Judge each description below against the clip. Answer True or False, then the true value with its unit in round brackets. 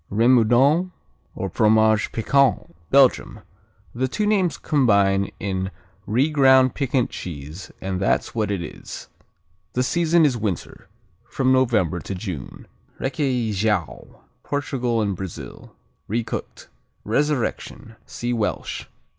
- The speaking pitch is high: False (115 Hz)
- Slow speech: True (110 wpm)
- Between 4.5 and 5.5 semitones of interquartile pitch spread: True (5.0 semitones)